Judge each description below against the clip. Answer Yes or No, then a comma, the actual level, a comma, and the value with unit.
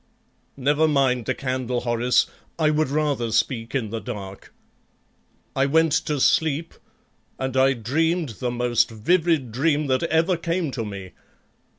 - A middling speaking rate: Yes, average, 145 wpm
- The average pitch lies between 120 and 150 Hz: Yes, low, 135 Hz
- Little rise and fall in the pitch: No, average, 4.7 semitones